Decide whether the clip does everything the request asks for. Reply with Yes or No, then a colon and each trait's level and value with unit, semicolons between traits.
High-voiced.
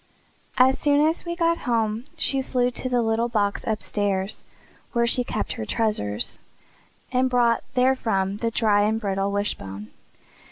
Yes: high, 225 Hz